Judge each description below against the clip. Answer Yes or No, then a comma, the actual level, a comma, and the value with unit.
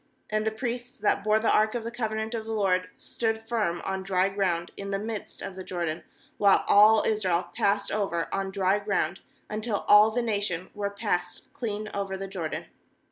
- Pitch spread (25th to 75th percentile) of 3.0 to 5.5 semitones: No, narrow, 2.4 semitones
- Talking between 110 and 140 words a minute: No, average, 190 wpm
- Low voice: No, high, 205 Hz